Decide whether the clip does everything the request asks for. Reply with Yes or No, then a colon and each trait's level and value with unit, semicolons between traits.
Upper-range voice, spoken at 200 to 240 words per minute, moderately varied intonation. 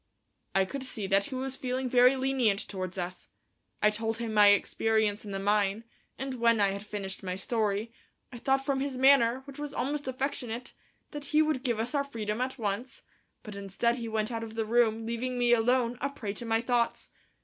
Yes: high, 230 Hz; fast, 205 wpm; average, 3.7 semitones